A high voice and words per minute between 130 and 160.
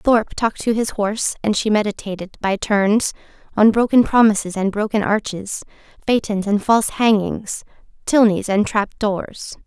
Yes: high, 210 Hz; average, 150 wpm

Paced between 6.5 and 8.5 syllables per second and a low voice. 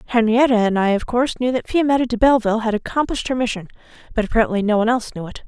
No: 7.9 syllables/s; high, 230 Hz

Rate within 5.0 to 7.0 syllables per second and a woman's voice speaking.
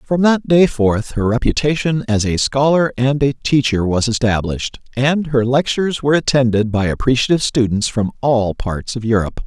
No: 5.2 syllables/s; male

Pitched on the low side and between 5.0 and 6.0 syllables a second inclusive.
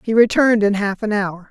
No: high, 210 Hz; 5.7 syllables/s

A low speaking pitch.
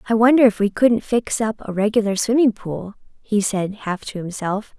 No: high, 210 Hz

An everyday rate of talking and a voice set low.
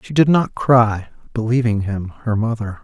Yes: average, 170 wpm; low, 115 Hz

